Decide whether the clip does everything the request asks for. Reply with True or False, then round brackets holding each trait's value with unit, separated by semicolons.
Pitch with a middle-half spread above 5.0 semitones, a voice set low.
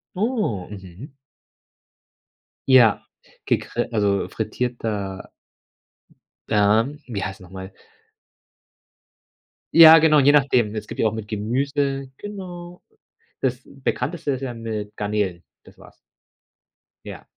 True (5.4 semitones; 120 Hz)